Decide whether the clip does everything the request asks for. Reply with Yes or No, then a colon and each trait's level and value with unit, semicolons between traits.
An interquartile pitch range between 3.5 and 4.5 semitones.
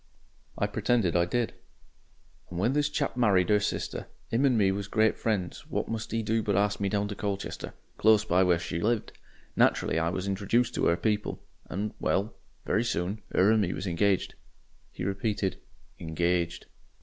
No: average, 3.1 semitones